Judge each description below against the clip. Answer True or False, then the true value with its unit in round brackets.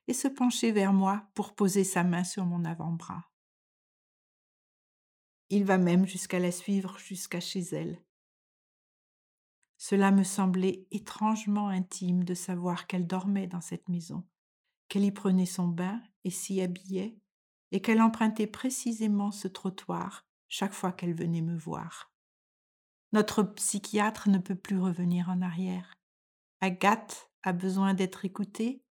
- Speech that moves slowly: True (135 wpm)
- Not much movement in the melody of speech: True (2.2 semitones)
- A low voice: False (190 Hz)